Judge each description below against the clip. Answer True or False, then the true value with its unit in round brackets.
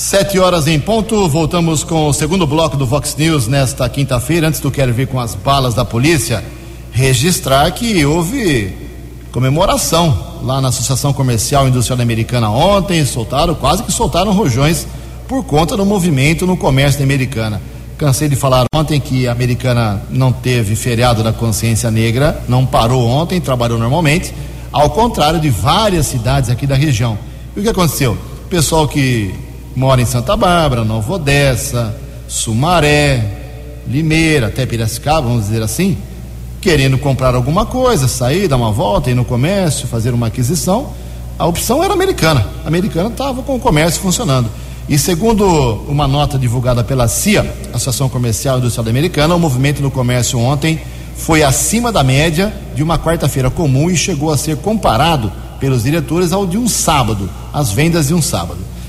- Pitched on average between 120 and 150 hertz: True (135 Hz)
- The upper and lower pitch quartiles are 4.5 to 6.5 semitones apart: True (5.0 semitones)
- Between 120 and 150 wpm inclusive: False (160 wpm)